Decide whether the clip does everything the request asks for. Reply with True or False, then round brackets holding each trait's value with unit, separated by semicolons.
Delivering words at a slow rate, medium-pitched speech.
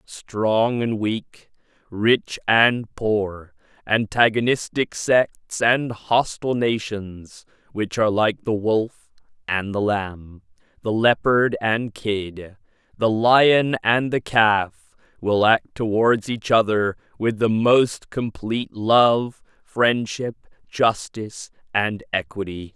False (105 wpm; 110 Hz)